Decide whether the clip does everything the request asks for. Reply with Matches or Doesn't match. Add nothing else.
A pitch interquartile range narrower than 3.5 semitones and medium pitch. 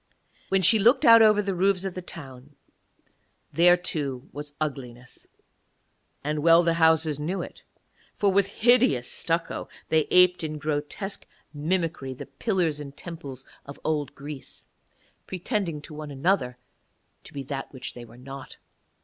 Doesn't match